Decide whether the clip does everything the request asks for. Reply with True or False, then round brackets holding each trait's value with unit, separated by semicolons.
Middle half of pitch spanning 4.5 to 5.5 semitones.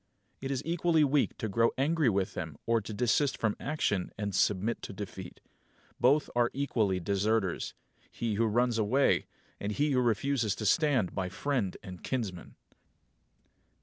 True (5.2 semitones)